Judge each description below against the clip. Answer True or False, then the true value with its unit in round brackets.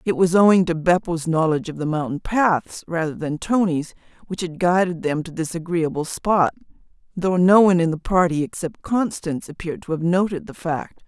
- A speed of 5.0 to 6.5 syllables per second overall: True (5.3 syllables/s)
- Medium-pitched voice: True (170 Hz)